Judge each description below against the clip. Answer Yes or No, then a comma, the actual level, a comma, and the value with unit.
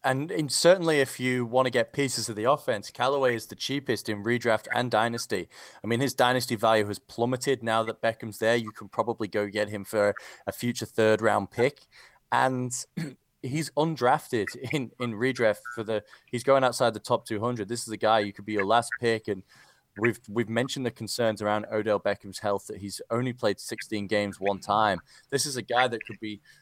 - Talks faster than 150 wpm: Yes, fast, 205 wpm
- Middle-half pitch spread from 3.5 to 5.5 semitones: No, average, 2.8 semitones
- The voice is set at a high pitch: No, low, 115 Hz